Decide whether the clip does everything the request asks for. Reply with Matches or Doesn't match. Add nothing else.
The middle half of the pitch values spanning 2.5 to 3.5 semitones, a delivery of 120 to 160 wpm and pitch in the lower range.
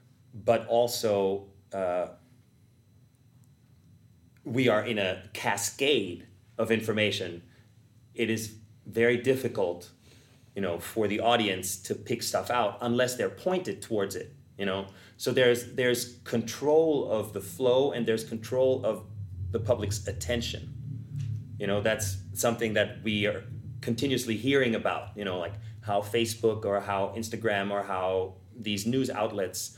Matches